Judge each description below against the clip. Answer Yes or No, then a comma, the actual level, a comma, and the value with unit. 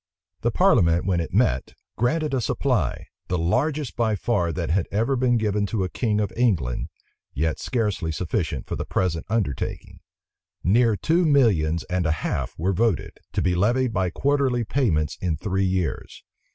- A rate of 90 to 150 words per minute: No, average, 165 wpm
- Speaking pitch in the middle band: No, low, 100 Hz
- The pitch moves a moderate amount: No, wide, 6.2 semitones